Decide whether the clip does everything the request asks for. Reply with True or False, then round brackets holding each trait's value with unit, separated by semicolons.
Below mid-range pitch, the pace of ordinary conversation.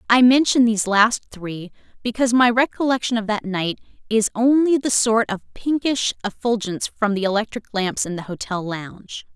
False (220 Hz; 165 wpm)